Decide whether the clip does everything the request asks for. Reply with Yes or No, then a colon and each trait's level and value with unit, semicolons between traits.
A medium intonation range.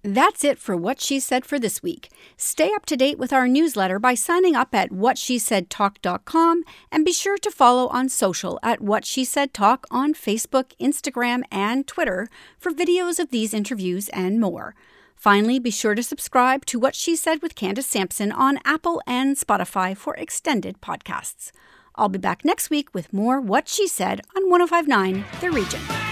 No: wide, 7.0 semitones